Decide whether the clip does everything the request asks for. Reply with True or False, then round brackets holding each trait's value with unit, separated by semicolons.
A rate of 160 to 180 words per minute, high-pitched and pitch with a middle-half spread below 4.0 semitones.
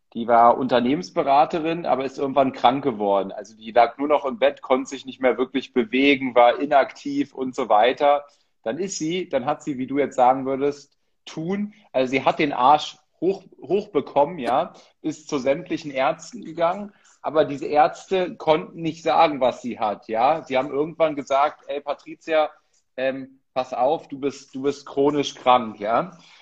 False (175 wpm; 140 Hz; 3.2 semitones)